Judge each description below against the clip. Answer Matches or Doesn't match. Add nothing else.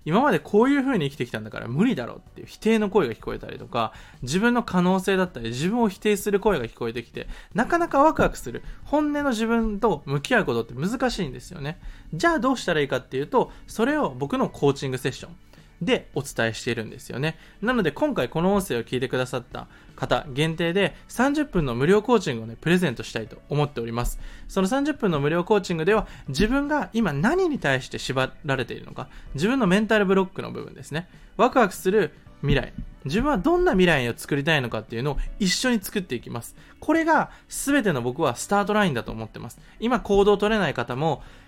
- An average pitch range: Doesn't match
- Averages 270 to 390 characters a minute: Doesn't match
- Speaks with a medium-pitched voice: Matches